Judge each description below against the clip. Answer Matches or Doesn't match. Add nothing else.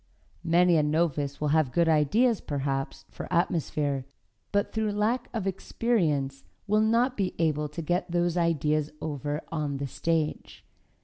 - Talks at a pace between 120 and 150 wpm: Matches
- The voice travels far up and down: Doesn't match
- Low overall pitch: Doesn't match